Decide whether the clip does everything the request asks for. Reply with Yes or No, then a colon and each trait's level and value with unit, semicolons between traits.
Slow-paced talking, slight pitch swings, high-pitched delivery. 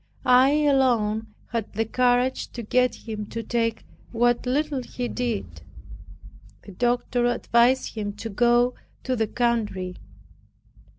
Yes: slow, 125 wpm; narrow, 2.1 semitones; high, 240 Hz